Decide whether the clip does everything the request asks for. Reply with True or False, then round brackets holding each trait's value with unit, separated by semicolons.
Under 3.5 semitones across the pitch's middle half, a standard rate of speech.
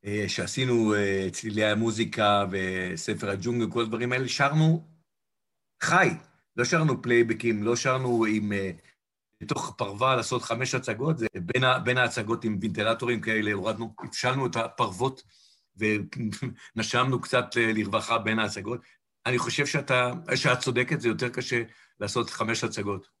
True (2.7 semitones; 125 wpm)